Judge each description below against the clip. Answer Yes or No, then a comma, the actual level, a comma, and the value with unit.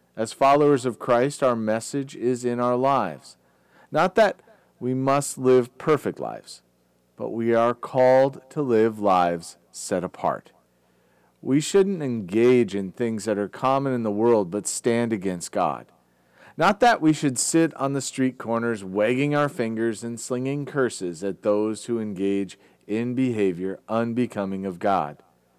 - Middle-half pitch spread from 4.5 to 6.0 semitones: Yes, average, 4.8 semitones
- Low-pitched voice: Yes, low, 115 Hz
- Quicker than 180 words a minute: No, average, 150 wpm